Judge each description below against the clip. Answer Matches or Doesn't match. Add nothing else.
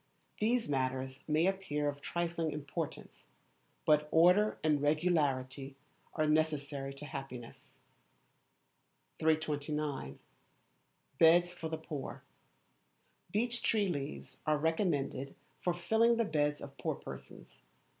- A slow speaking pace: Matches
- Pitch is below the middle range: Doesn't match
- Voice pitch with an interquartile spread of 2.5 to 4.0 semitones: Matches